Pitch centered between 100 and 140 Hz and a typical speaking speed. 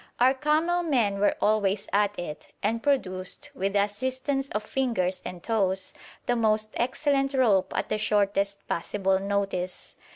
No: high, 210 Hz; average, 150 wpm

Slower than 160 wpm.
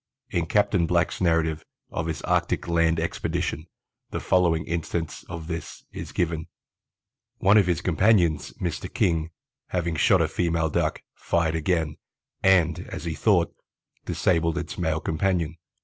Yes: average, 140 wpm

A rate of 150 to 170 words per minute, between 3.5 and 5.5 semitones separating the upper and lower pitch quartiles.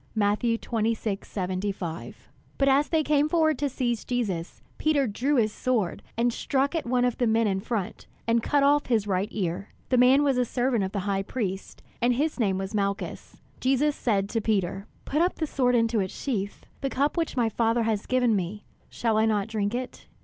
No: average, 200 wpm; average, 4.5 semitones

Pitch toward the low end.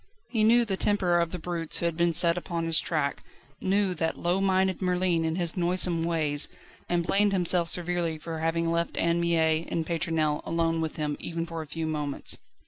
No: medium, 170 Hz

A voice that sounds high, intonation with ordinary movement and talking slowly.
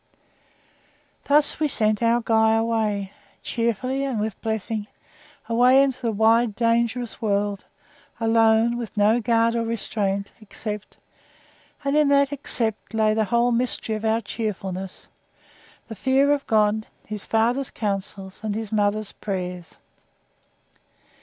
No: high, 225 Hz; narrow, 2.1 semitones; slow, 125 wpm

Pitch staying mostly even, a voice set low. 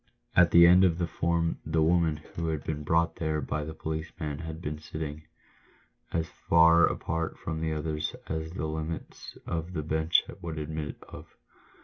Yes: narrow, 1.2 semitones; very low, 80 Hz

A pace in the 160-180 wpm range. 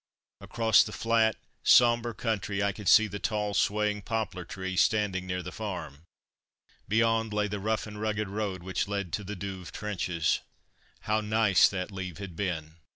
Yes: average, 165 wpm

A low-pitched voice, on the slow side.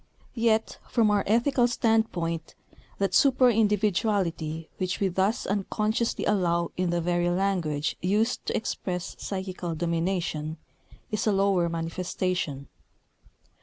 No: medium, 185 Hz; slow, 115 wpm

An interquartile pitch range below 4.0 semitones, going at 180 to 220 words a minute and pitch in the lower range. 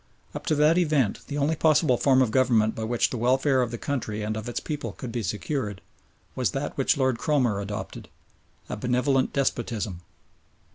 No: average, 4.4 semitones; average, 185 wpm; low, 125 Hz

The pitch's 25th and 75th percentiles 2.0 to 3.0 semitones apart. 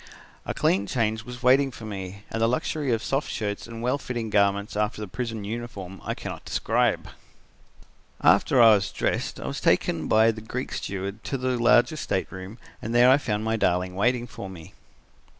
No: average, 3.4 semitones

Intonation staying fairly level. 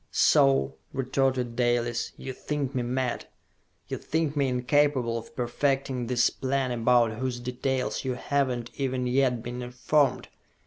Yes: narrow, 1.9 semitones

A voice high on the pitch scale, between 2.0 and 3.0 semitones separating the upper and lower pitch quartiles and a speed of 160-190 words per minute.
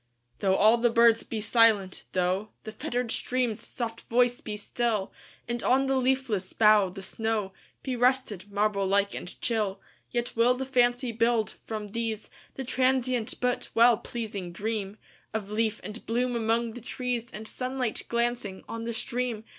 No: high, 230 Hz; narrow, 2.5 semitones; average, 140 wpm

